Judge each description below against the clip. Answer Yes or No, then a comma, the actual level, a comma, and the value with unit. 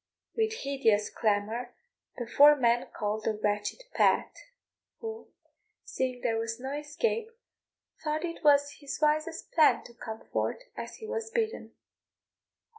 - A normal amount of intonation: No, wide, 6.6 semitones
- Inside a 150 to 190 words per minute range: No, slow, 135 wpm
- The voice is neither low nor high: No, very high, 280 Hz